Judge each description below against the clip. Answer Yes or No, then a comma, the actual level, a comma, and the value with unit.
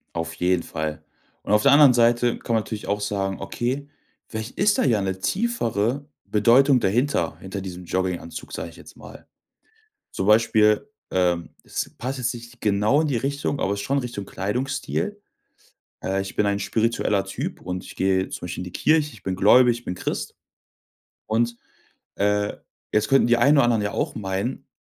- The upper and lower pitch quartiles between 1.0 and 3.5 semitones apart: No, average, 4.6 semitones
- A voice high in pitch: No, low, 110 Hz